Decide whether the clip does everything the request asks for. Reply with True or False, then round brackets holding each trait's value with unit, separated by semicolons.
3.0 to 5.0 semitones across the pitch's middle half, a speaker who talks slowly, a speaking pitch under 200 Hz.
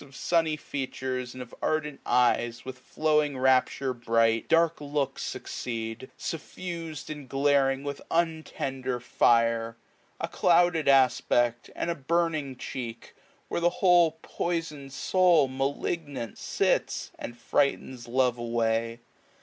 True (4.5 semitones; 120 wpm; 135 Hz)